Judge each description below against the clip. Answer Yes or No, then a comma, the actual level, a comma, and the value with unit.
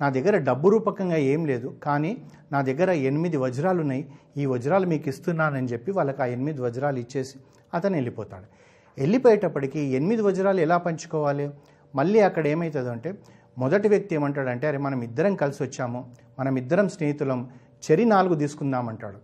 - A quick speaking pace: Yes, fast, 140 wpm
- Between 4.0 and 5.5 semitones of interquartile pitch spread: Yes, average, 4.6 semitones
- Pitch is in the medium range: Yes, medium, 145 Hz